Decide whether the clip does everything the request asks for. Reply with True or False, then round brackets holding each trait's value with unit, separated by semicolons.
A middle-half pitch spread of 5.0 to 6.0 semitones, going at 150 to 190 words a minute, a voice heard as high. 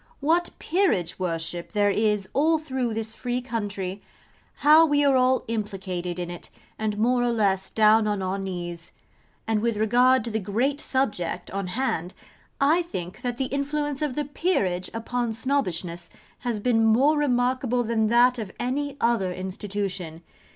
True (5.3 semitones; 155 wpm; 225 Hz)